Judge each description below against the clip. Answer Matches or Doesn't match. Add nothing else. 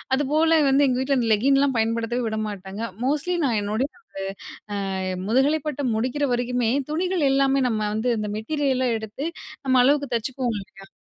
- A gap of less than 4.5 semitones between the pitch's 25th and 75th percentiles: Matches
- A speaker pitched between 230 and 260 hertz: Matches